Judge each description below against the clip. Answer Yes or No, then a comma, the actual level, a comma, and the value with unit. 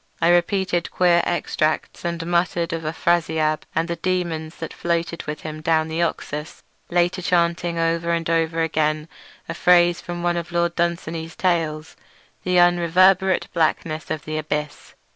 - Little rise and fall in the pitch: Yes, narrow, 1.5 semitones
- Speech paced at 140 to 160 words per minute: Yes, average, 145 wpm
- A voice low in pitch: No, medium, 170 Hz